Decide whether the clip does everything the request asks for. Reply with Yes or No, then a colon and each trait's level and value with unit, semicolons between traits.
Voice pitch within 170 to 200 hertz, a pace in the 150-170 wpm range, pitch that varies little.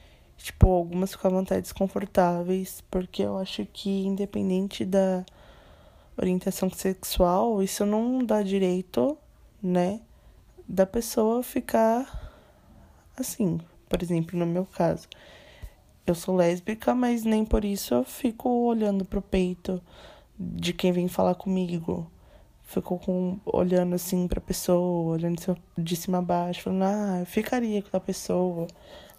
No: medium, 185 Hz; average, 125 wpm; narrow, 2.3 semitones